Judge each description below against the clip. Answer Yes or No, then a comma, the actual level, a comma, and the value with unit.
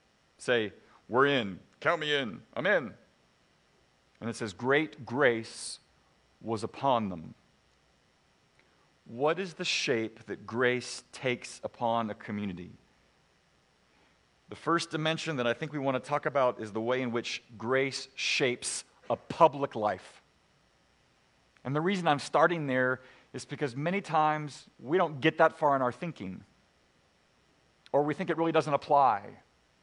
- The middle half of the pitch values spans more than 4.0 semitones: Yes, average, 5.1 semitones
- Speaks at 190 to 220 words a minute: No, average, 145 wpm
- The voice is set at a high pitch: No, low, 130 Hz